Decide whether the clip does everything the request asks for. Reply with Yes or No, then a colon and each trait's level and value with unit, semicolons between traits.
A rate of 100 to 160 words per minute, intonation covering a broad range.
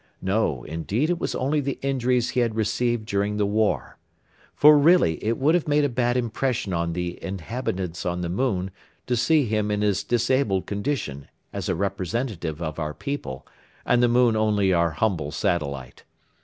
No: average, 175 wpm; wide, 6.1 semitones